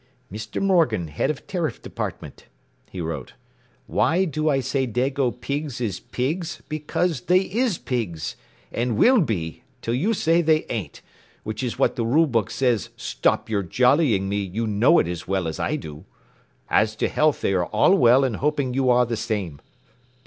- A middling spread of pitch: No, wide, 6.5 semitones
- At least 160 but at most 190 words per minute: Yes, average, 180 wpm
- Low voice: Yes, low, 125 Hz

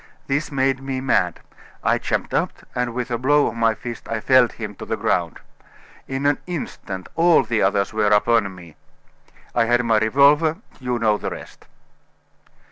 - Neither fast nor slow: Yes, average, 175 wpm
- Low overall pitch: Yes, low, 120 Hz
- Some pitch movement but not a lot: Yes, average, 3.9 semitones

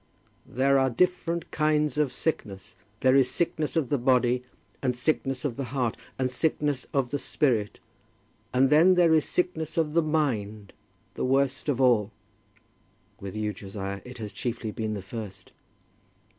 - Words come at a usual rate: Yes, average, 155 wpm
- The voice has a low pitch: Yes, low, 130 Hz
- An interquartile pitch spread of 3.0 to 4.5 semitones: No, average, 5.1 semitones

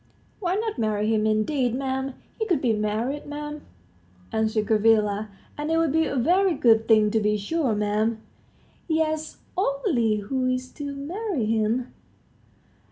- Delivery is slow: No, average, 150 wpm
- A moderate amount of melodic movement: No, wide, 5.8 semitones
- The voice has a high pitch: Yes, very high, 255 Hz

